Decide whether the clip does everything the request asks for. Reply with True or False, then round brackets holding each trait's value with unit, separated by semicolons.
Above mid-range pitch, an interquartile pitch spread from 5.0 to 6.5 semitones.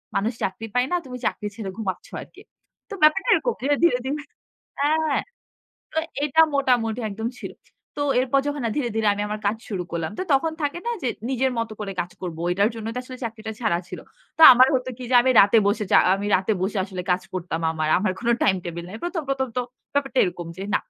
True (230 Hz; 5.5 semitones)